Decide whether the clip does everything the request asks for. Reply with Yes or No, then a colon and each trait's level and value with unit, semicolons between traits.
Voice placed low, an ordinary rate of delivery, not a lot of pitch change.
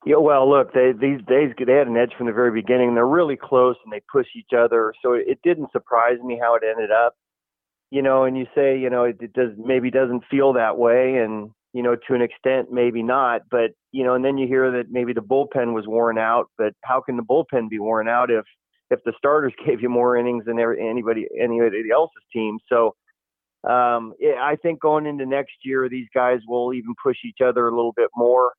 No: low, 125 Hz; fast, 230 wpm; narrow, 2.0 semitones